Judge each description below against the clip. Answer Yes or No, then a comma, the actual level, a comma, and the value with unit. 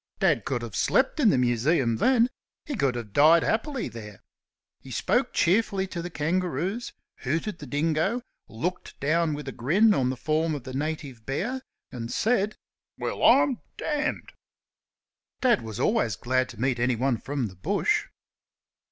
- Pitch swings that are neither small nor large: No, wide, 7.9 semitones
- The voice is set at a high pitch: No, medium, 150 Hz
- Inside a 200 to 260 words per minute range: No, average, 160 wpm